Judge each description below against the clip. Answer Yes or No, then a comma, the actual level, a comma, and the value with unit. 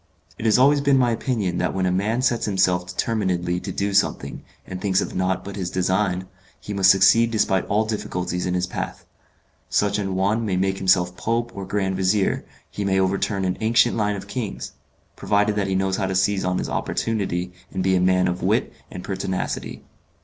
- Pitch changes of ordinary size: No, narrow, 2.2 semitones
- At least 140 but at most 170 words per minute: No, average, 200 wpm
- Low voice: Yes, very low, 95 Hz